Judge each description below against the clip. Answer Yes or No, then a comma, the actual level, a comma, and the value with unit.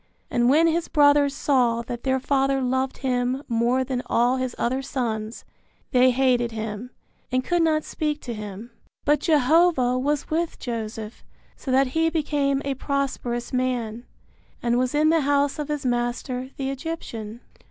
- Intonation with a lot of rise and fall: No, average, 3.0 semitones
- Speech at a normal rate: Yes, average, 160 wpm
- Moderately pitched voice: No, very high, 260 Hz